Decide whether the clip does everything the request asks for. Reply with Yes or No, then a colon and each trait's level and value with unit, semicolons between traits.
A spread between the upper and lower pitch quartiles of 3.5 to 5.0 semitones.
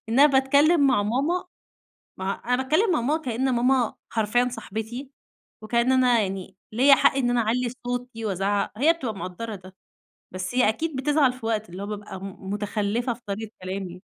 Yes: average, 4.3 semitones